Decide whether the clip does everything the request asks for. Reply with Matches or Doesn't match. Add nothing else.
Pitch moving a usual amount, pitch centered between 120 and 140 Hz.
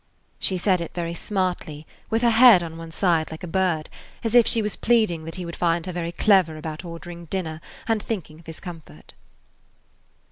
Doesn't match